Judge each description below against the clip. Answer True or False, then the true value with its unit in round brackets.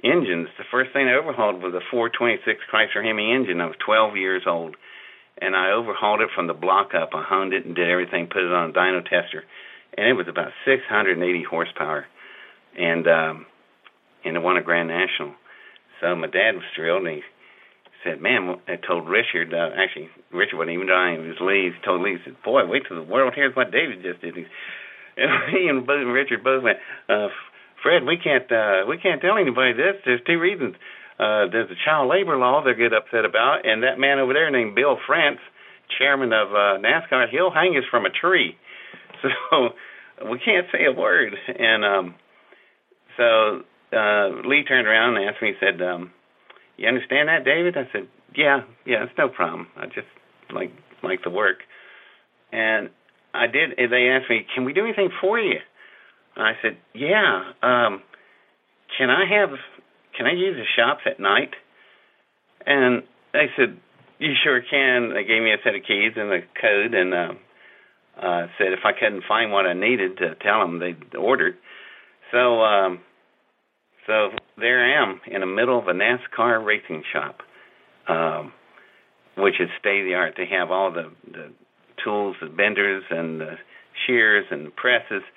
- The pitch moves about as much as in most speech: False (5.9 semitones)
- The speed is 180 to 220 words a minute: True (190 wpm)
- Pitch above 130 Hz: False (105 Hz)